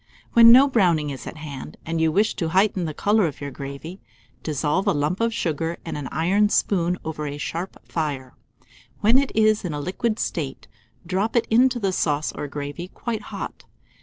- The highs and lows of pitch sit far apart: Yes, wide, 6.0 semitones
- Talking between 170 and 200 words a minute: Yes, average, 190 wpm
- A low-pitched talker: No, medium, 170 Hz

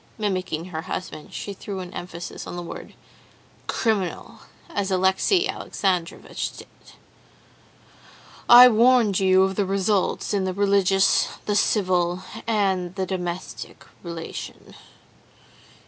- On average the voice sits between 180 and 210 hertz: Yes, high, 190 Hz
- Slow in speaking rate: Yes, slow, 115 wpm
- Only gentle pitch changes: Yes, narrow, 2.2 semitones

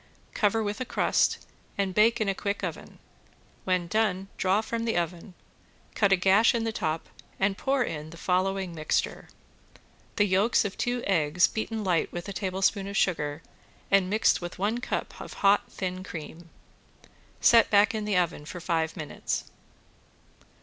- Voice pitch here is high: Yes, high, 195 Hz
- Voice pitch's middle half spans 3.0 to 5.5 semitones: Yes, average, 3.3 semitones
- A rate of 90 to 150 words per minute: No, average, 165 wpm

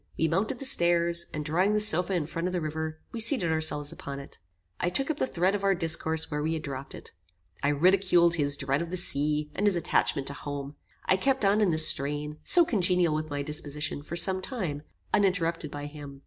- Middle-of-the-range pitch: Yes, medium, 165 Hz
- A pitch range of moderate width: Yes, average, 4.0 semitones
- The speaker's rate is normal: No, fast, 220 wpm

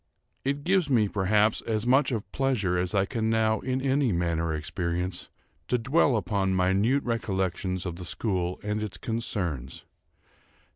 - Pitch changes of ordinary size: Yes, average, 4.9 semitones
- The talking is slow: No, average, 150 wpm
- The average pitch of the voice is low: Yes, low, 105 Hz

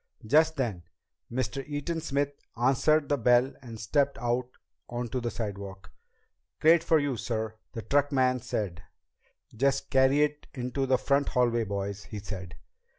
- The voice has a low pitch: Yes, low, 125 Hz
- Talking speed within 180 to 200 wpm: No, average, 145 wpm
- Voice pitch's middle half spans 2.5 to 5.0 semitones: Yes, average, 4.2 semitones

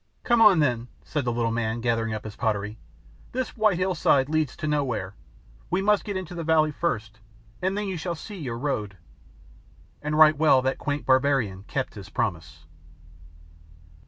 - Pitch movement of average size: No, wide, 6.9 semitones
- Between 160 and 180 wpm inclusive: Yes, average, 170 wpm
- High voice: No, medium, 140 Hz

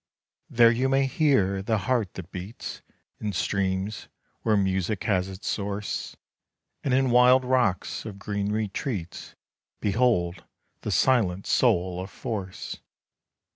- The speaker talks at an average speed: No, slow, 125 wpm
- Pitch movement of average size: Yes, average, 4.3 semitones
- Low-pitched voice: Yes, low, 105 Hz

